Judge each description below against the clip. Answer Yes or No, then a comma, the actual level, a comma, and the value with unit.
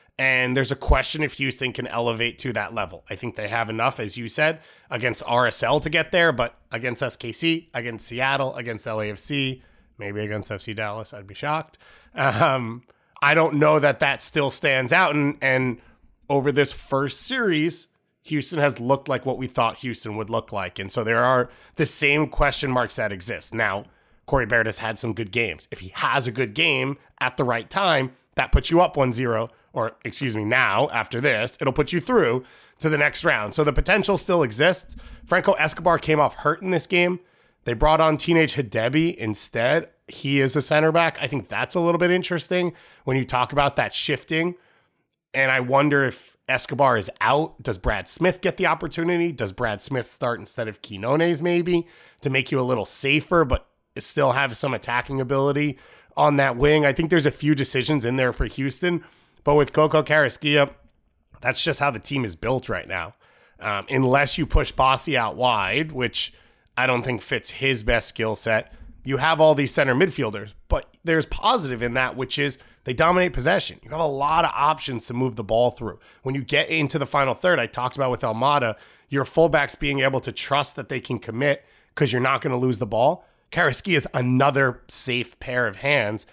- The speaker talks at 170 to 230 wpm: Yes, average, 200 wpm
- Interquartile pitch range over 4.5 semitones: No, average, 4.0 semitones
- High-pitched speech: No, low, 135 Hz